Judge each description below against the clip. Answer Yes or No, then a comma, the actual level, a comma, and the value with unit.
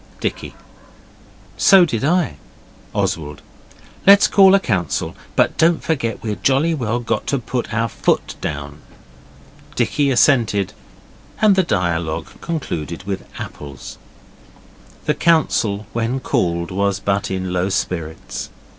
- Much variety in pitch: Yes, wide, 8.3 semitones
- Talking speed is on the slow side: Yes, slow, 120 wpm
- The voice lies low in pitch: Yes, low, 105 Hz